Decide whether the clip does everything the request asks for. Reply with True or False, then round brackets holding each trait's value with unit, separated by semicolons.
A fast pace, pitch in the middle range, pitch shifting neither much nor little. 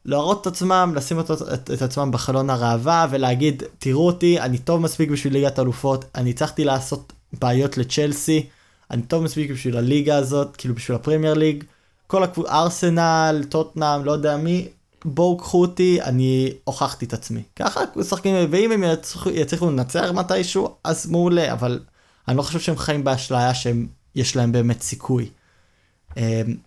True (160 wpm; 145 Hz; 4.7 semitones)